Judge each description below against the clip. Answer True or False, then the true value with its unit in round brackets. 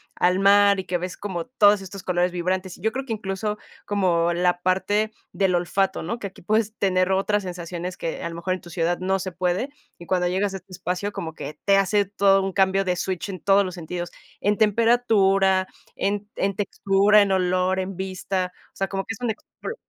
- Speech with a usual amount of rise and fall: False (1.9 semitones)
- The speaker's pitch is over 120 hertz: True (190 Hz)